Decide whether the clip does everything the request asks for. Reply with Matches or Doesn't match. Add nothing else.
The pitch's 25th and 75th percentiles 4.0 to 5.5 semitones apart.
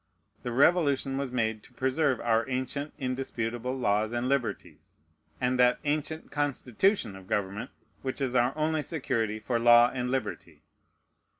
Doesn't match